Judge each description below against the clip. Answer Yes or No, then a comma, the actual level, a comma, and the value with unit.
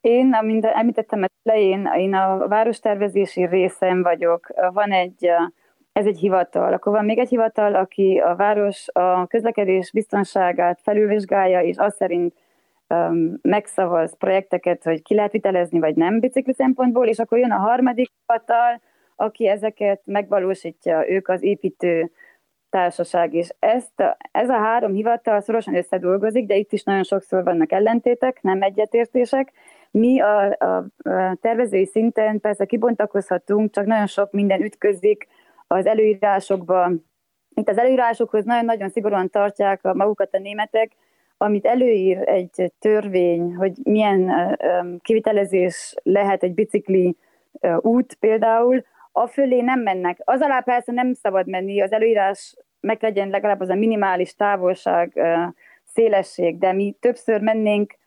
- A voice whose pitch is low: No, high, 205 Hz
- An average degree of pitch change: Yes, average, 3.3 semitones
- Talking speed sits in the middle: Yes, average, 135 wpm